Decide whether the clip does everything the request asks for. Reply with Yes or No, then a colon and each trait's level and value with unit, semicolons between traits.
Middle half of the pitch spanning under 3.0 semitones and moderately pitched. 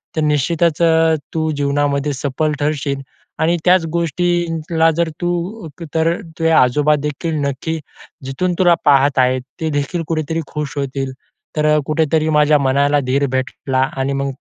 Yes: narrow, 2.6 semitones; medium, 150 Hz